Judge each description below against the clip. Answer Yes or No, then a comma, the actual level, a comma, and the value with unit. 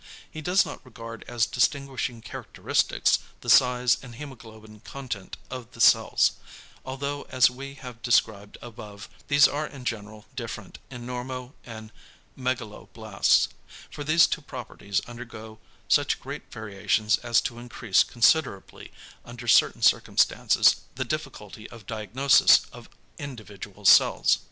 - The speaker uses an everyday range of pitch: Yes, average, 3.1 semitones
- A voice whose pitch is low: Yes, low, 120 Hz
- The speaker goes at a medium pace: No, slow, 125 wpm